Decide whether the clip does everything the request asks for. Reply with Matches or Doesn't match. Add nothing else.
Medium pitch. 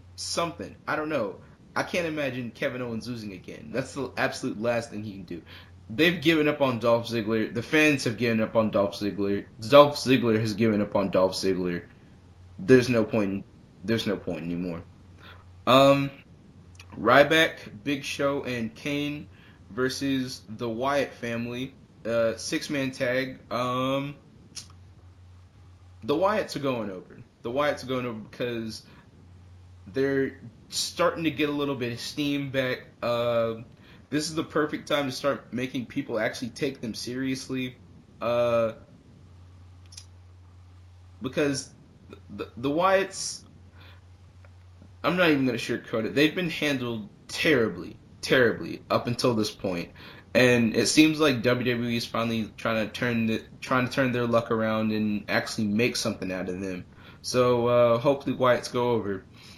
Doesn't match